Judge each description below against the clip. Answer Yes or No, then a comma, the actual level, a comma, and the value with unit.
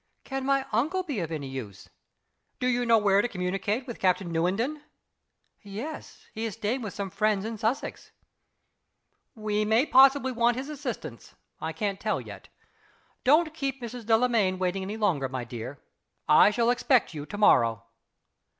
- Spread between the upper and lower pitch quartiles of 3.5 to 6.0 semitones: Yes, average, 5.1 semitones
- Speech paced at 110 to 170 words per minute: Yes, average, 160 wpm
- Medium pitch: No, high, 215 Hz